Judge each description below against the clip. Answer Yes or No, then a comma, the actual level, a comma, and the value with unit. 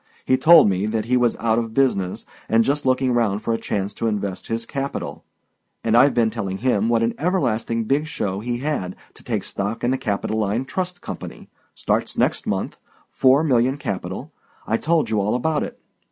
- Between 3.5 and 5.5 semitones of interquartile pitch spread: Yes, average, 4.0 semitones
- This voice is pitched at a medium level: No, low, 115 Hz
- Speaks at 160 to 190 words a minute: Yes, average, 180 wpm